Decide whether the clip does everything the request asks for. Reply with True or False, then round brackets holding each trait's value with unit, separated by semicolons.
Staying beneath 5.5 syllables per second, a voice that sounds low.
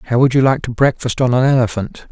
False (5.8 syllables/s; 125 Hz)